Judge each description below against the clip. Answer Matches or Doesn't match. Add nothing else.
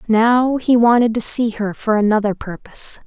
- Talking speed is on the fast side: Doesn't match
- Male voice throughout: Doesn't match